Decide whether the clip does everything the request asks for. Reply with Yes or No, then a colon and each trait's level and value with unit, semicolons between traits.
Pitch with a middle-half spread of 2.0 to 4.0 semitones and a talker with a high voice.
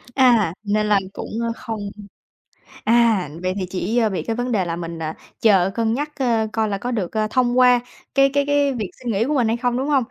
Yes: average, 3.6 semitones; high, 225 Hz